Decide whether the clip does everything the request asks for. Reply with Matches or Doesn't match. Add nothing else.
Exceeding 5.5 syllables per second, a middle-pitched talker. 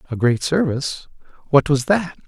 Doesn't match